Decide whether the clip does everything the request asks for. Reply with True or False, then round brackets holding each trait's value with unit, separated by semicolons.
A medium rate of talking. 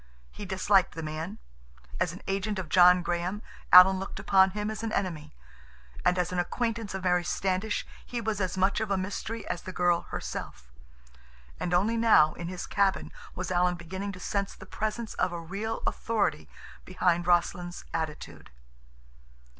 True (170 wpm)